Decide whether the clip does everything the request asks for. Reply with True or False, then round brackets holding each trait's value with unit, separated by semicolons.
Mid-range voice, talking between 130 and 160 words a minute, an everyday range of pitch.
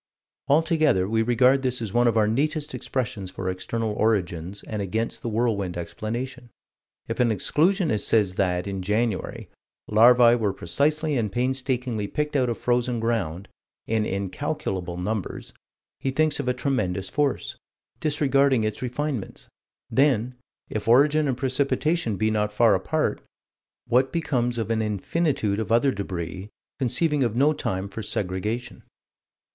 False (115 Hz; 140 wpm; 4.7 semitones)